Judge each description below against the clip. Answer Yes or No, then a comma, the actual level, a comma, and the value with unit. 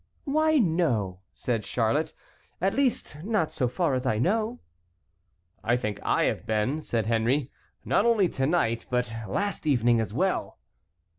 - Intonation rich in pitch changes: Yes, wide, 8.6 semitones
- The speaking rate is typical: Yes, average, 150 wpm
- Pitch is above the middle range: No, medium, 140 Hz